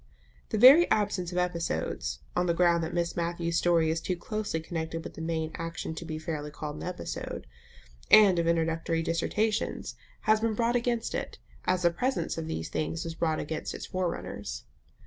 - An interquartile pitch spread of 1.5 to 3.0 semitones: Yes, narrow, 2.4 semitones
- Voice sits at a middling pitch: Yes, medium, 170 Hz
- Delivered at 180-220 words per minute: Yes, average, 185 wpm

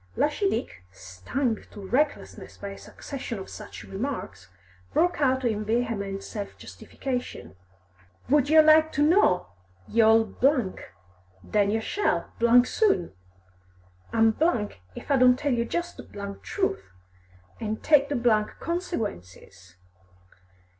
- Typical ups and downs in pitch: No, wide, 6.3 semitones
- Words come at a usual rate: No, slow, 115 wpm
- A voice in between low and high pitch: No, high, 235 Hz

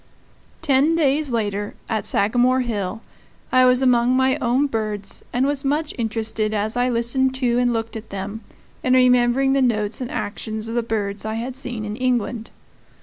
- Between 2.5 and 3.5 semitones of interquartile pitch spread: Yes, average, 2.9 semitones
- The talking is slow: No, average, 175 wpm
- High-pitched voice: Yes, high, 240 Hz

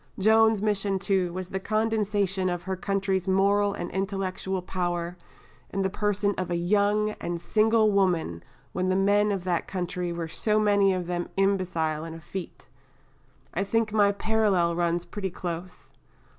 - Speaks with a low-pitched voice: No, high, 190 Hz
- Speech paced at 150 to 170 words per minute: Yes, average, 160 wpm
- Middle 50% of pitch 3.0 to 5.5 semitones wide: No, narrow, 2.5 semitones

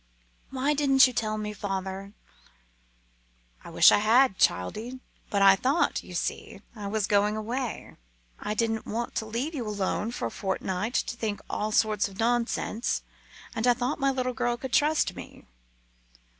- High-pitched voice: Yes, high, 225 Hz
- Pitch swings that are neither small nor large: Yes, average, 3.5 semitones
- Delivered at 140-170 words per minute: Yes, average, 165 wpm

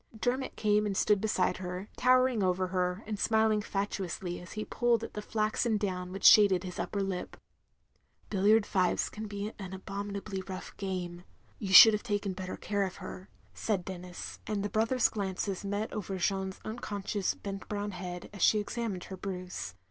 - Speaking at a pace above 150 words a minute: Yes, average, 180 wpm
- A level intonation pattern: Yes, narrow, 2.3 semitones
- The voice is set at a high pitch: Yes, high, 200 Hz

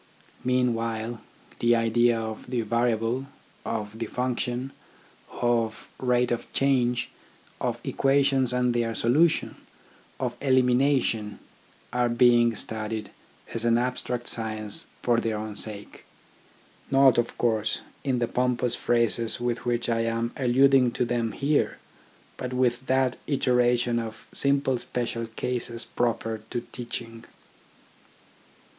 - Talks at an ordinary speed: No, slow, 120 wpm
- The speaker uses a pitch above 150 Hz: No, low, 120 Hz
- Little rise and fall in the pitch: Yes, narrow, 1.7 semitones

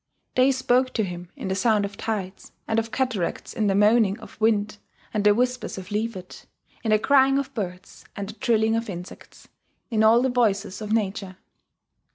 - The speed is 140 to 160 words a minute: No, average, 190 wpm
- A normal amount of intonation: Yes, average, 3.1 semitones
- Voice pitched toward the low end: No, high, 215 Hz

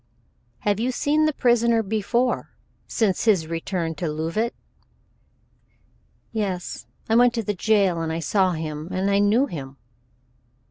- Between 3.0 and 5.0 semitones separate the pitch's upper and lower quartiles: No, wide, 5.6 semitones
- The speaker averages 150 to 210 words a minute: No, average, 140 wpm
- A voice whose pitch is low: No, high, 200 Hz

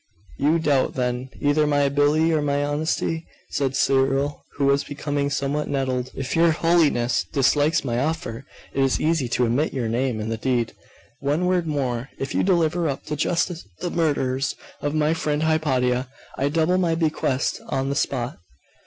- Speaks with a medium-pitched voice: Yes, medium, 145 Hz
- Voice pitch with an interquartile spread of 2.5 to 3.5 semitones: Yes, average, 3.2 semitones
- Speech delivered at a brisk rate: No, average, 170 wpm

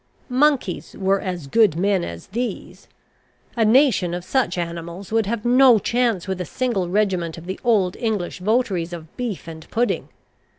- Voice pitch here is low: No, high, 195 Hz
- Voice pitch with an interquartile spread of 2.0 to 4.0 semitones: No, average, 5.0 semitones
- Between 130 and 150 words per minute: No, average, 165 wpm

